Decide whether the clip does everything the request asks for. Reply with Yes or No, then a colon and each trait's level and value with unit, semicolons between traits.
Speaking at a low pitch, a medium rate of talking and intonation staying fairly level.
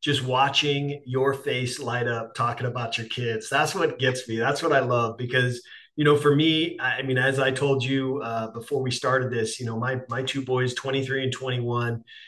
No: low, 130 Hz; fast, 210 wpm; narrow, 2.2 semitones